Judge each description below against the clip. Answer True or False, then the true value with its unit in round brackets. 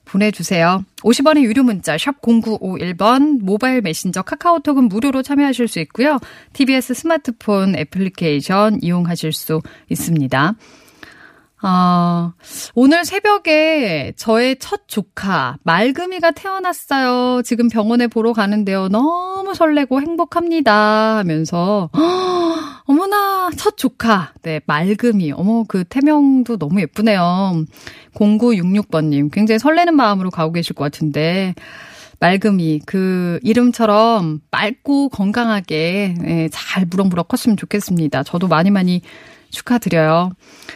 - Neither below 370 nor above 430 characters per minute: False (270 characters per minute)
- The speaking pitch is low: False (215 Hz)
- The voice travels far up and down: True (7.3 semitones)